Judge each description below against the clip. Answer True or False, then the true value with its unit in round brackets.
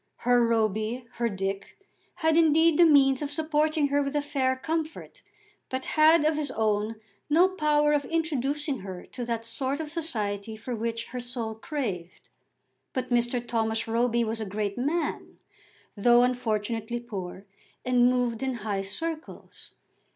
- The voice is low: False (245 Hz)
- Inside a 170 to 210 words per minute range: False (150 wpm)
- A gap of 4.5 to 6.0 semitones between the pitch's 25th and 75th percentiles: True (5.0 semitones)